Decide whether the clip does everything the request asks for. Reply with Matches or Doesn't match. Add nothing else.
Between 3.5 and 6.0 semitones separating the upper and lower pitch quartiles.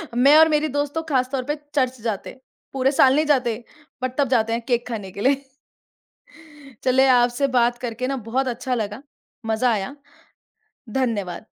Doesn't match